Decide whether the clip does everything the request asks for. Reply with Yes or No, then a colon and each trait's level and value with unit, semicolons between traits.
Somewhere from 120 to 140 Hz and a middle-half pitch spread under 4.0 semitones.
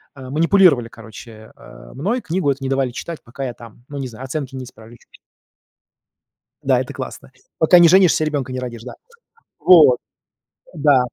No: low, 135 Hz; average, 4.4 semitones